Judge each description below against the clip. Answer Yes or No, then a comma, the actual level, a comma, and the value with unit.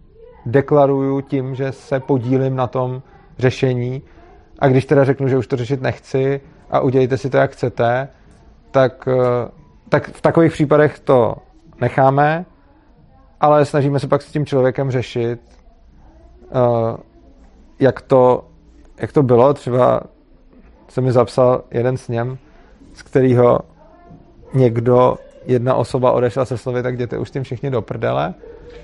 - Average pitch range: No, narrow, 1.9 semitones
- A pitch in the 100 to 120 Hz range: No, low, 130 Hz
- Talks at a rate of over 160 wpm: No, average, 135 wpm